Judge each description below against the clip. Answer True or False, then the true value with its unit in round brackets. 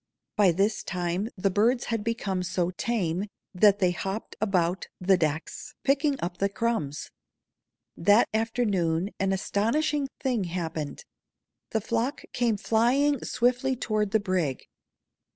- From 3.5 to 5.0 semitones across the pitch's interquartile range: True (4.3 semitones)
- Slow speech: True (130 wpm)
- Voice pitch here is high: True (205 Hz)